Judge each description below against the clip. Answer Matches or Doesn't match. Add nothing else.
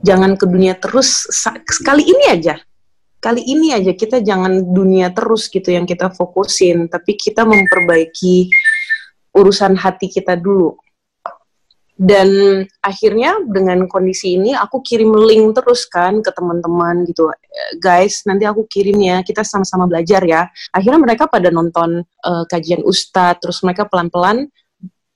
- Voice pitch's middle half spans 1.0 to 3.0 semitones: Doesn't match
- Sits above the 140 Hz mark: Matches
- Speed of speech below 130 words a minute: Doesn't match